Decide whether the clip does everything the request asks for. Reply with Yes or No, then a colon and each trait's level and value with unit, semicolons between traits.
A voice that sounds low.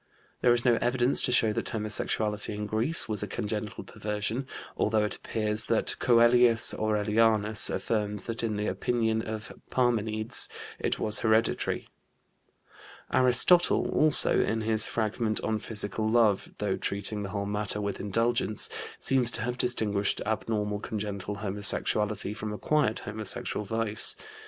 Yes: low, 110 Hz